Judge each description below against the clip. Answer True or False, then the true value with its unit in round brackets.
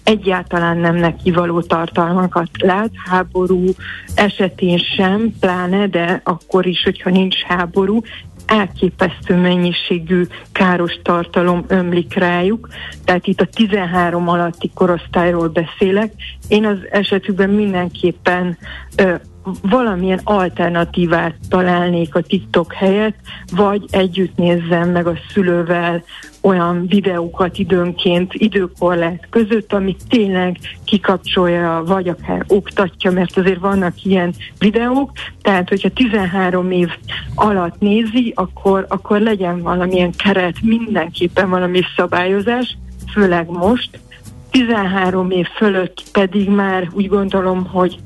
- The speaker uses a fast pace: False (105 wpm)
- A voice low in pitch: False (185 Hz)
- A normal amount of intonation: False (2.1 semitones)